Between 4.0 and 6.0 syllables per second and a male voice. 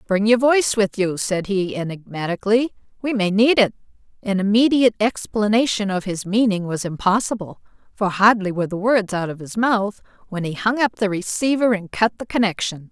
No: 5.4 syllables/s; female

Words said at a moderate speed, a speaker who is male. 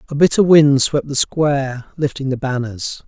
Yes: average, 175 wpm; male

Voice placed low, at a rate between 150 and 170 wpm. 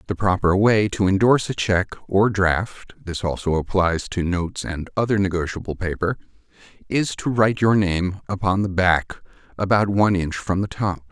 Yes: very low, 95 Hz; average, 160 wpm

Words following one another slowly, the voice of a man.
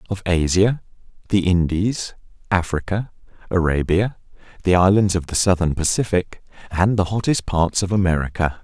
Yes: slow, 125 wpm; male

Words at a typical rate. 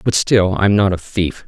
No: fast, 245 wpm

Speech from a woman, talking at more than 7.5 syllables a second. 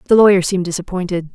Yes: female; 8.0 syllables/s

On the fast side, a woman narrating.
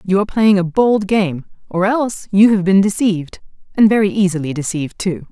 No: average, 190 wpm; female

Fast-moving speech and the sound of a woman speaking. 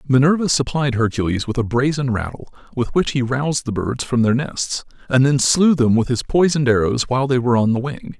No: fast, 220 wpm; male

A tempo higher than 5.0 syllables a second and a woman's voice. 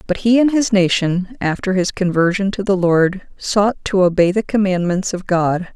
No: 4.7 syllables/s; female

